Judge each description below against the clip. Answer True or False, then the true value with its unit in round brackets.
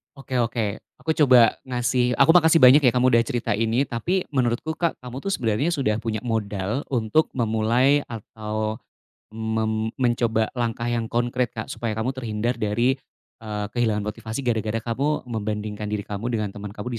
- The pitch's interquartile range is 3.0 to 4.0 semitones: False (2.6 semitones)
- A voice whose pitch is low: True (115 Hz)